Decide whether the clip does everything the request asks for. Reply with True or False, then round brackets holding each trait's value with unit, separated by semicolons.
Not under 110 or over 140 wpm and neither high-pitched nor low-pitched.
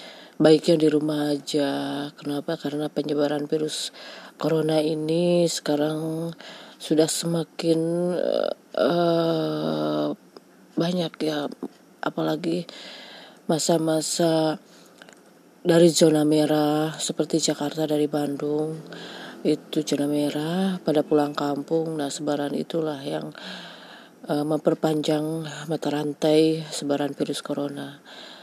False (90 wpm; 155 Hz)